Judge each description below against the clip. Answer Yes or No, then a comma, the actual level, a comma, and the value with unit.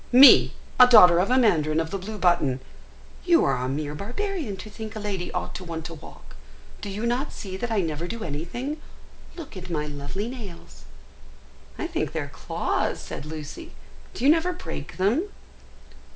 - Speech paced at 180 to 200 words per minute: Yes, average, 185 wpm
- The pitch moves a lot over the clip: Yes, wide, 7.1 semitones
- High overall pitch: Yes, high, 195 Hz